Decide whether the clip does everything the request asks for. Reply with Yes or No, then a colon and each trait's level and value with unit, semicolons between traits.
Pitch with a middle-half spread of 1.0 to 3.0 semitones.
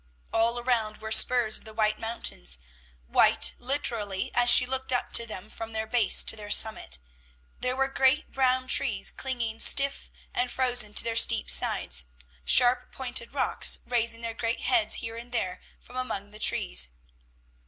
Yes: average, 2.7 semitones